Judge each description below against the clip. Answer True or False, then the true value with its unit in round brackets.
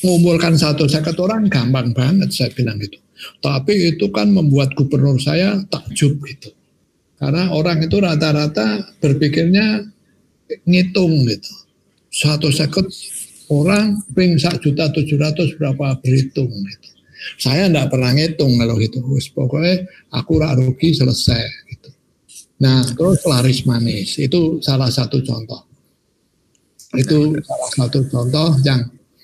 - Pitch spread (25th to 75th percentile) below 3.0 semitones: False (4.7 semitones)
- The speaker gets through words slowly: False (125 wpm)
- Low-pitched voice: False (145 Hz)